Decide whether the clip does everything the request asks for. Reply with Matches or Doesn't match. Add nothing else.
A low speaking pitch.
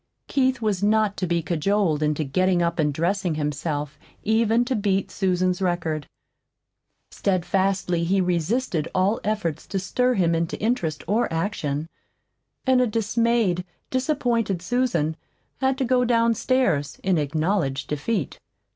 Doesn't match